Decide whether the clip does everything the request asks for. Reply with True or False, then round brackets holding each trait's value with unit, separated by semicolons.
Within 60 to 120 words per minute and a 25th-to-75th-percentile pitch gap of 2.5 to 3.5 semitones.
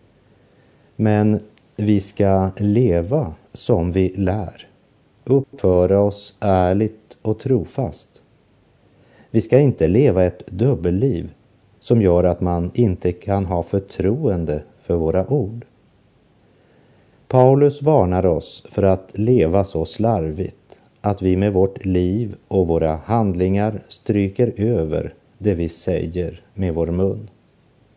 False (115 wpm; 4.0 semitones)